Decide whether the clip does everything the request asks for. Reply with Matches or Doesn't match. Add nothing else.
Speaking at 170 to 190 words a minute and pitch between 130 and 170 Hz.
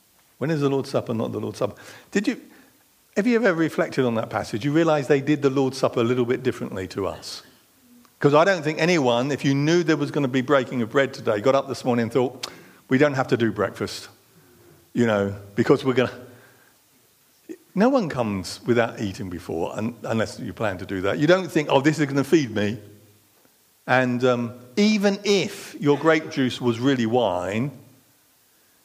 Doesn't match